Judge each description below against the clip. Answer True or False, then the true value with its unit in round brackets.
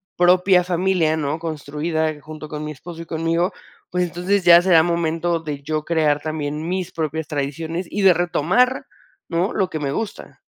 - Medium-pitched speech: True (165 Hz)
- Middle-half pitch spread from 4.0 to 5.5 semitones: False (2.4 semitones)